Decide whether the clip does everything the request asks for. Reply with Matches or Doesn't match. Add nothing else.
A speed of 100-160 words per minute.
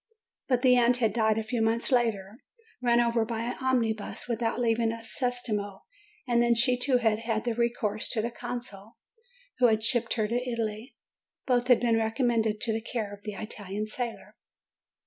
Doesn't match